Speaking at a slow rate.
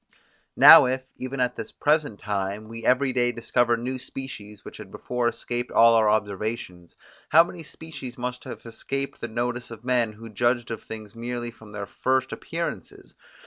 No: average, 175 wpm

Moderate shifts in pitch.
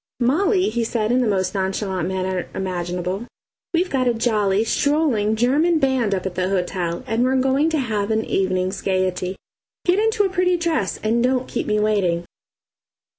No: wide, 5.9 semitones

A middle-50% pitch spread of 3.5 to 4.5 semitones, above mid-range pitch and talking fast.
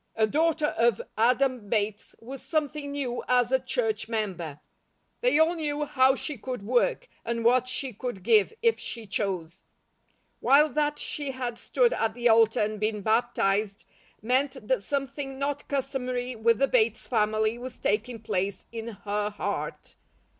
No: average, 4.1 semitones; high, 245 Hz; average, 155 wpm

